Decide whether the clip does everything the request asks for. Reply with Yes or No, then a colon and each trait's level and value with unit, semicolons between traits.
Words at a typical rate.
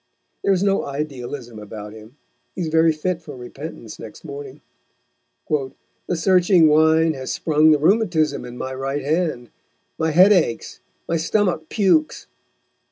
Yes: average, 145 wpm